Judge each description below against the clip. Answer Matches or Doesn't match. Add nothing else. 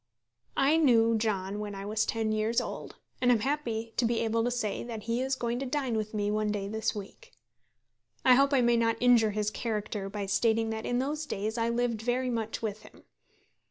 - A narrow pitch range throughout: Matches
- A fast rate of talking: Matches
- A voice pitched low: Doesn't match